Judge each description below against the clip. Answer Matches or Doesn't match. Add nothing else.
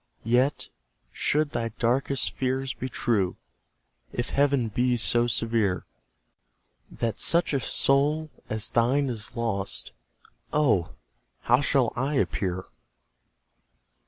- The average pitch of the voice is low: Matches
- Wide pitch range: Doesn't match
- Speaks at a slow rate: Matches